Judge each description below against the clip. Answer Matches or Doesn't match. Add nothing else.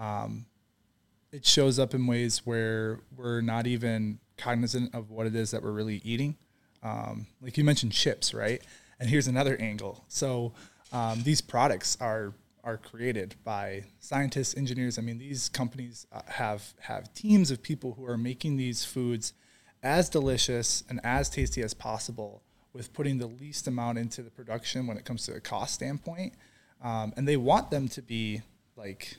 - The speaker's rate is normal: Matches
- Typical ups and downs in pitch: Matches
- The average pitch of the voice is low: Matches